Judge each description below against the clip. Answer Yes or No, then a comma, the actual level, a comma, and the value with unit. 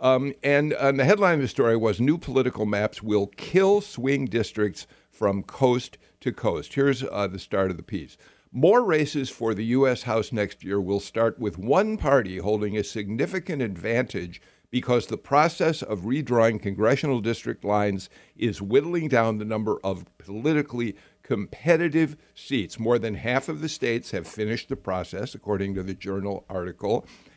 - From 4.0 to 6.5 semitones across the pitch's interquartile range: Yes, average, 5.2 semitones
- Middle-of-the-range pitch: No, low, 115 Hz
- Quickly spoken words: No, average, 165 wpm